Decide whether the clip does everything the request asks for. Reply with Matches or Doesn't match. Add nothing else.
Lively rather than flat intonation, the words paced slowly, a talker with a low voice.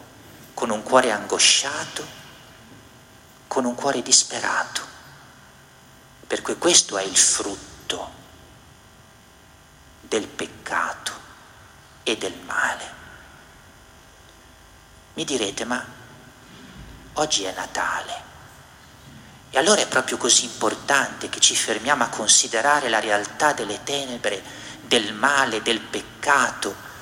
Matches